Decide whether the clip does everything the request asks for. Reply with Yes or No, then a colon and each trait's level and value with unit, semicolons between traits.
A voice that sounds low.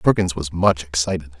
Yes: very low, 85 Hz